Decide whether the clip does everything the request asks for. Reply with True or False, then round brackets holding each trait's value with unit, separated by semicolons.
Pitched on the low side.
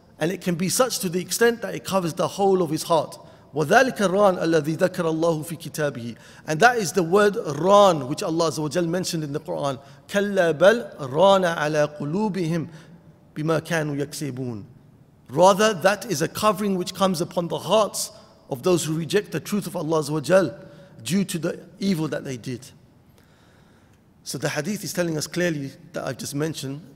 False (170 Hz)